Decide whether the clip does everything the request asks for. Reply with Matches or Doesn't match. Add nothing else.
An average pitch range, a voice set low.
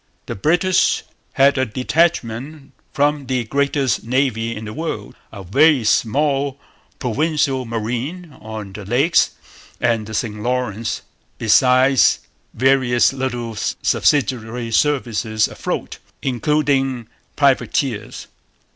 Matches